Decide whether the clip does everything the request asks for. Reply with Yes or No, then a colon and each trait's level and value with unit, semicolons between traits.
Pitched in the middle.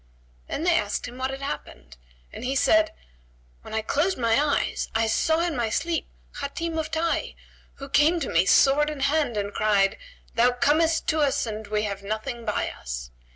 No: very high, 270 Hz